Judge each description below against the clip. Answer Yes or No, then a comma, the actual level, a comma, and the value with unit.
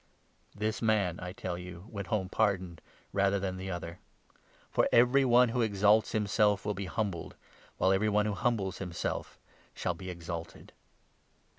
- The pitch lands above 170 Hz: No, low, 100 Hz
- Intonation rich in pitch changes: No, average, 2.9 semitones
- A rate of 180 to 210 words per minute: No, average, 160 wpm